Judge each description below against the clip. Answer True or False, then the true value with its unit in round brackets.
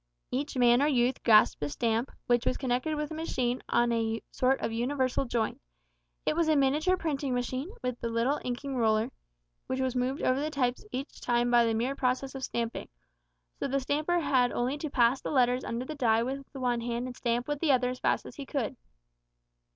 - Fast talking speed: True (215 wpm)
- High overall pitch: True (255 Hz)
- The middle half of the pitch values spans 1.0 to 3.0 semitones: True (2.5 semitones)